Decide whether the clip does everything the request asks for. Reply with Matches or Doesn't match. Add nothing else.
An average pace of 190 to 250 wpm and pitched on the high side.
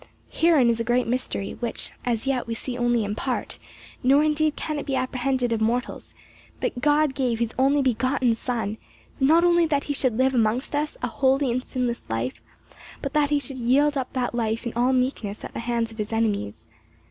Matches